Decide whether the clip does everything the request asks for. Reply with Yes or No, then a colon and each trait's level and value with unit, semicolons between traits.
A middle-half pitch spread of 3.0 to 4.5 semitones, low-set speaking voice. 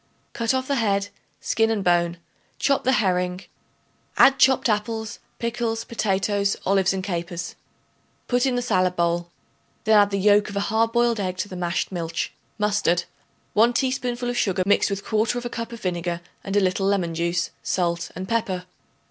No: average, 4.1 semitones; high, 200 Hz